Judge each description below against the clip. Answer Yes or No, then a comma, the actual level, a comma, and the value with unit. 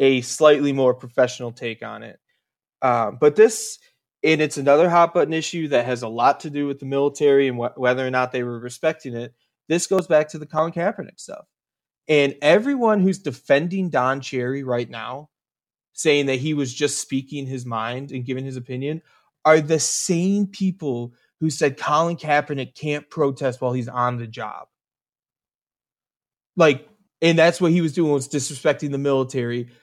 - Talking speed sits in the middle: Yes, average, 175 wpm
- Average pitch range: Yes, average, 3.8 semitones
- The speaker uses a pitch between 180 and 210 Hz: No, medium, 140 Hz